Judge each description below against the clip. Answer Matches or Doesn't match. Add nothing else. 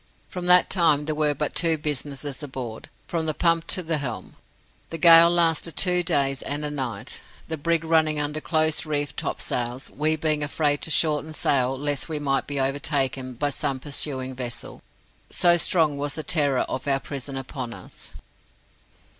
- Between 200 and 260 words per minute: Doesn't match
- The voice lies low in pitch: Doesn't match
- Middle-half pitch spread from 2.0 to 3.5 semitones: Matches